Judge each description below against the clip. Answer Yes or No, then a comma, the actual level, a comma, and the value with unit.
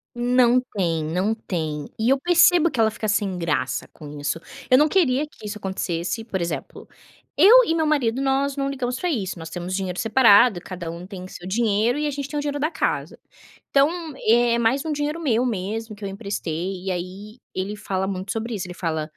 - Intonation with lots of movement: Yes, wide, 6.5 semitones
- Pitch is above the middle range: Yes, high, 215 Hz